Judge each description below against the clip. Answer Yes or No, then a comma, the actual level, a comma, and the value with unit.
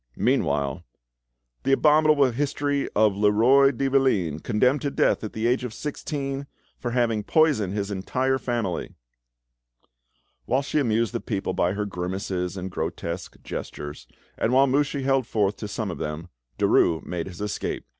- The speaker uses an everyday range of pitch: No, wide, 6.0 semitones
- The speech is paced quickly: No, average, 155 wpm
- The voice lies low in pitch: Yes, low, 115 Hz